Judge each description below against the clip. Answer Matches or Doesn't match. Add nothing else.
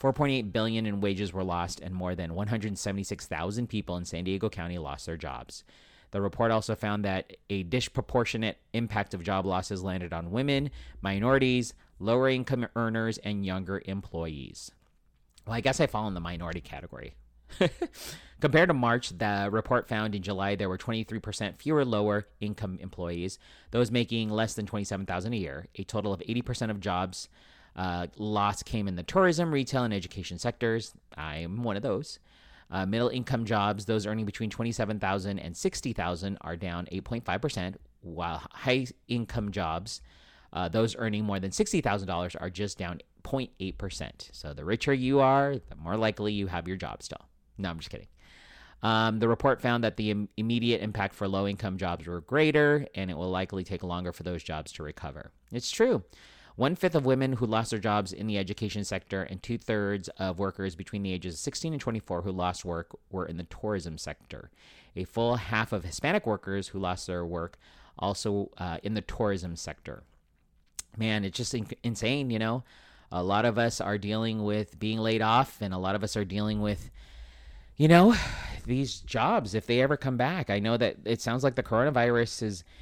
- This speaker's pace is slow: Doesn't match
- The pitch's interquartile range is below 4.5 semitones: Matches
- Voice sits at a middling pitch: Doesn't match